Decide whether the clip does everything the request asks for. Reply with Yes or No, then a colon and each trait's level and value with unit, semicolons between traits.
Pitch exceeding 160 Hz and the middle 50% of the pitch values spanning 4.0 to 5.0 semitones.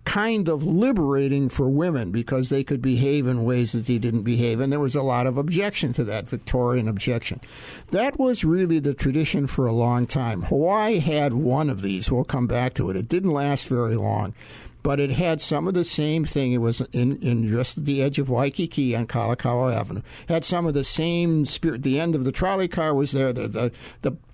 No: low, 135 Hz; average, 4.4 semitones